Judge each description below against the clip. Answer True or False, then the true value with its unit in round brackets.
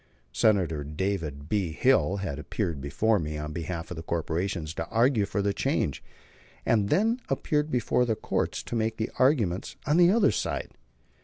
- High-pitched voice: False (100 Hz)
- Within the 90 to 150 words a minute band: False (175 wpm)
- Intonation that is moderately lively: False (6.5 semitones)